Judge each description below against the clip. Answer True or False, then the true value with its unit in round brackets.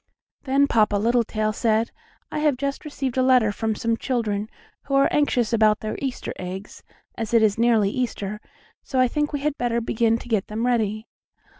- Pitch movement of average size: True (3.2 semitones)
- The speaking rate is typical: True (185 wpm)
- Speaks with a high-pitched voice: True (230 Hz)